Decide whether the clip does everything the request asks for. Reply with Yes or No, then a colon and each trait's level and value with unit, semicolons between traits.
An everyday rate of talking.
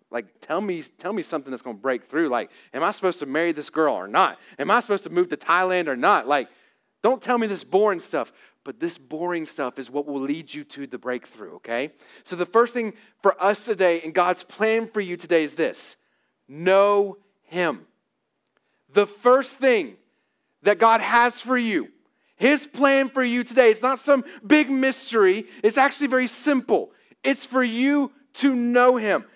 Yes: average, 195 wpm